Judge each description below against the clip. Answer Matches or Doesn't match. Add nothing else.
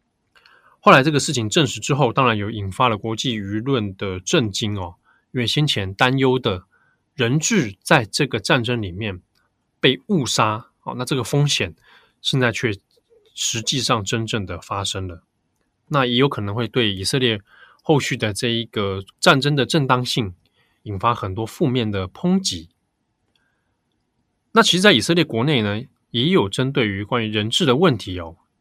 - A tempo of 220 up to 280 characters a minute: Matches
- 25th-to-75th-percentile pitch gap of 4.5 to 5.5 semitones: Matches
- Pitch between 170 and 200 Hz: Doesn't match